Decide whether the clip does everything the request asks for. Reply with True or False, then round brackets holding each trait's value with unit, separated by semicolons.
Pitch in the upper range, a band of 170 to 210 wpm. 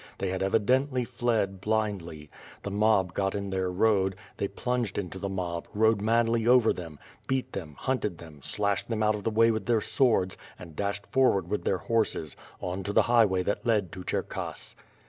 False (100 Hz; 185 wpm)